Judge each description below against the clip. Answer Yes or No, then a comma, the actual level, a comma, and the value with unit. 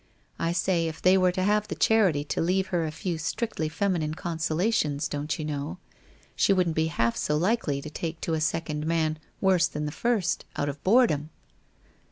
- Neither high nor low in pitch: Yes, medium, 165 Hz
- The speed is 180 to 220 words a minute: Yes, average, 200 wpm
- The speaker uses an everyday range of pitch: Yes, average, 3.5 semitones